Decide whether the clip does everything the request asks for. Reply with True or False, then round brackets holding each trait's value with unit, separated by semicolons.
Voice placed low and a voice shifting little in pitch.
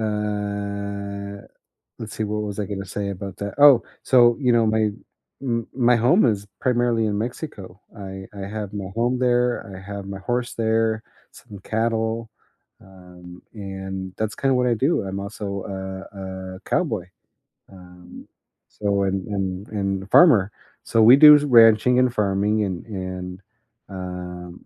False (105 Hz; 3.1 semitones)